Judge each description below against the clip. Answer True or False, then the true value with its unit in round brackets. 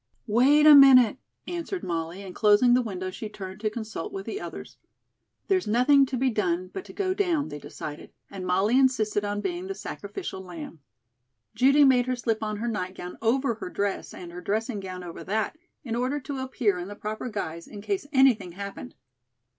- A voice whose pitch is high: True (220 Hz)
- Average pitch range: False (5.7 semitones)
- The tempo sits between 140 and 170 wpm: False (195 wpm)